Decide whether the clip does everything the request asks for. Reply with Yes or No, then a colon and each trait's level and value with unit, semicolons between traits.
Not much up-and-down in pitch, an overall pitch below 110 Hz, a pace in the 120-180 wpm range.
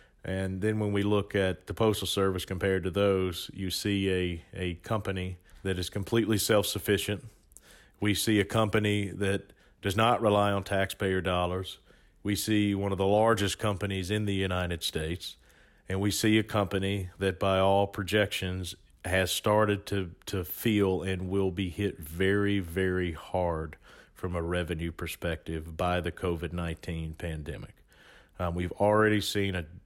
Yes: narrow, 2.2 semitones; very low, 95 Hz; average, 160 wpm